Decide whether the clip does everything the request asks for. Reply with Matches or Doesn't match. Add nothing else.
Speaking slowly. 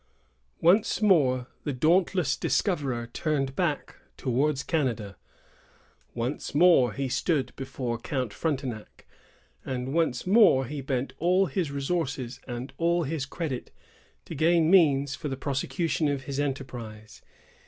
Matches